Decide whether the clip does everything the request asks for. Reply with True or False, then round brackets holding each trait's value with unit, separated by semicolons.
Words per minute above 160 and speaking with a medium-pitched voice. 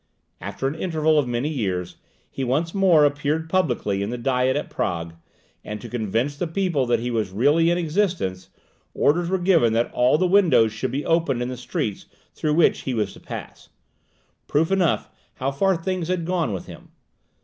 True (195 wpm; 145 Hz)